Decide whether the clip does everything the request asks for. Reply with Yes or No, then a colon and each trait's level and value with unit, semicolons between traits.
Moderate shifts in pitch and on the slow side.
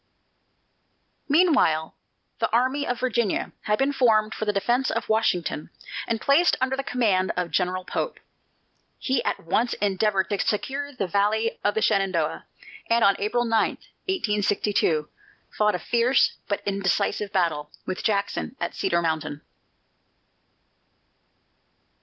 Yes: average, 4.5 semitones; slow, 130 wpm